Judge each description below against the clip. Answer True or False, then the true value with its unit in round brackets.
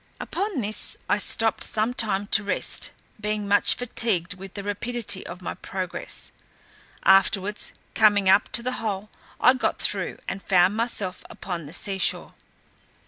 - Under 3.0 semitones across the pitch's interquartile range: True (2.6 semitones)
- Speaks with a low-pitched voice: False (205 Hz)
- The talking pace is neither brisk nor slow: True (150 wpm)